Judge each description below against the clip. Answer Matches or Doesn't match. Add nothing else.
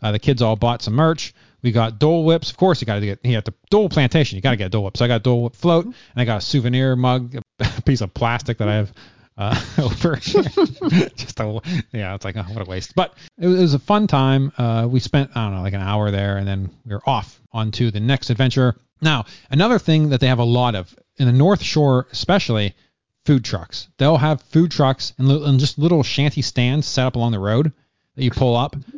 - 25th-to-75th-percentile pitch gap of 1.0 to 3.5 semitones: Doesn't match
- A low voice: Matches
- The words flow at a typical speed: Doesn't match